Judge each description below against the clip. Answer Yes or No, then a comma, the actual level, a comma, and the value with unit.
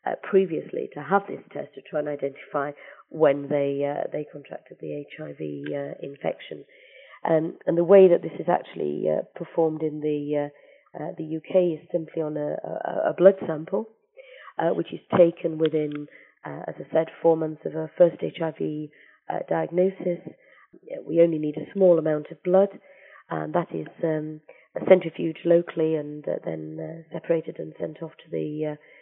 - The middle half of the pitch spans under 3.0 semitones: Yes, narrow, 2.6 semitones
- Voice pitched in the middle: Yes, medium, 160 Hz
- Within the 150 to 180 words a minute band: Yes, average, 175 wpm